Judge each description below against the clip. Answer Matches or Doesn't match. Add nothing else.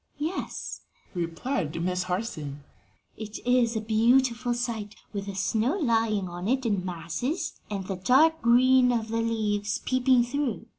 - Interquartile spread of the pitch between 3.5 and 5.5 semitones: Matches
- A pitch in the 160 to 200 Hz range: Doesn't match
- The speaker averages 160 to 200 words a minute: Doesn't match